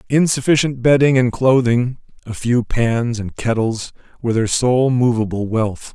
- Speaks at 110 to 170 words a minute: Yes, average, 140 wpm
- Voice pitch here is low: Yes, low, 120 Hz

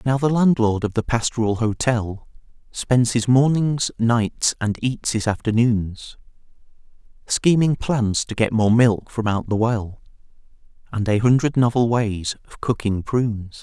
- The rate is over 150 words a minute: No, average, 145 wpm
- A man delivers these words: Yes, male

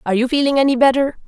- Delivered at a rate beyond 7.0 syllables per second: Yes, 8.3 syllables/s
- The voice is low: No, very high, 260 Hz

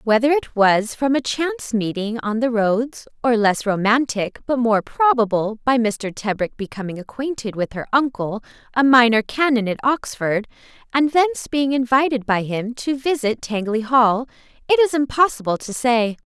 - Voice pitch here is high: Yes, high, 240 Hz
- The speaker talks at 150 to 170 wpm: Yes, average, 160 wpm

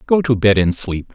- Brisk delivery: Yes, fast, 260 wpm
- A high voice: No, low, 115 Hz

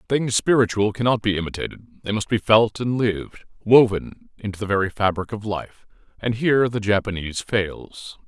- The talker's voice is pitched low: Yes, low, 105 Hz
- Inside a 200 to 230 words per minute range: No, average, 165 wpm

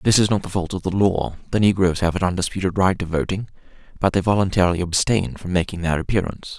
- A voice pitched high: No, very low, 95 Hz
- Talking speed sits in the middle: No, fast, 220 wpm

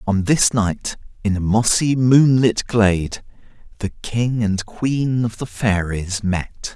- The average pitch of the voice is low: Yes, low, 110 Hz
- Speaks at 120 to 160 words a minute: Yes, average, 140 wpm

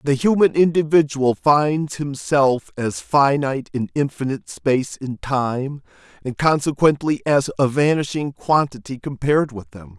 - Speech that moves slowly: Yes, slow, 125 wpm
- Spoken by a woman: No, male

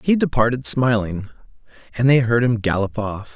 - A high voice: No, low, 115 Hz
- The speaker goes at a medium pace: Yes, average, 160 wpm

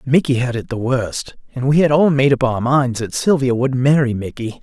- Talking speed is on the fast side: Yes, fast, 235 wpm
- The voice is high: No, low, 130 Hz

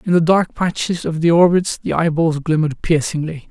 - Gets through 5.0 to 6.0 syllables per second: Yes, 5.3 syllables/s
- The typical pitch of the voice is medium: Yes, medium, 165 Hz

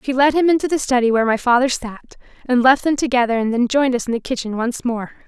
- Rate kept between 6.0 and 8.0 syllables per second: Yes, 6.5 syllables/s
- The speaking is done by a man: No, female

